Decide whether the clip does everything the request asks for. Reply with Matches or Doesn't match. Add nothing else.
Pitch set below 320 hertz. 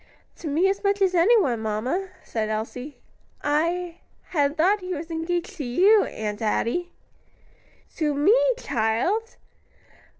Doesn't match